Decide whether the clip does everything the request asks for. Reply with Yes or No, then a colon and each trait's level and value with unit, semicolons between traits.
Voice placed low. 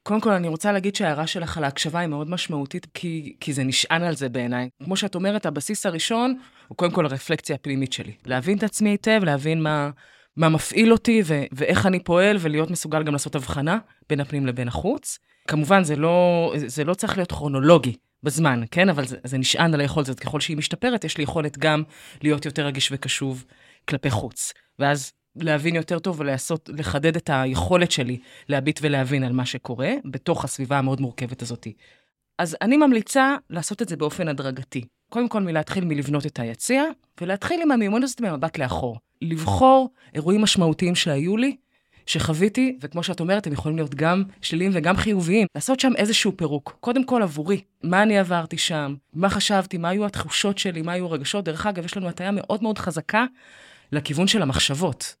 No: medium, 165 Hz